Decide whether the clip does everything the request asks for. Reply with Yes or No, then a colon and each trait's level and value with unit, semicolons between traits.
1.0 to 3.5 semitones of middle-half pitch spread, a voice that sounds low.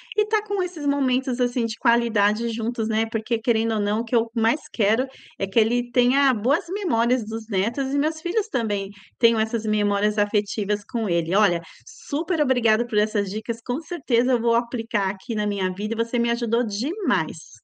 No: average, 3.2 semitones; high, 230 Hz